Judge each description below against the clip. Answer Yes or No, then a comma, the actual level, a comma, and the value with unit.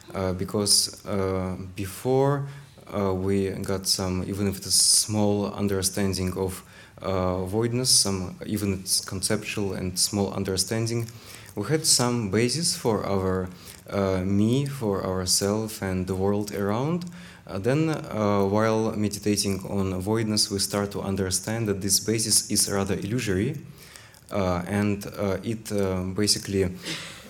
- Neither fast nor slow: No, slow, 130 wpm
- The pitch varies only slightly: Yes, narrow, 2.3 semitones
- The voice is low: Yes, low, 100 Hz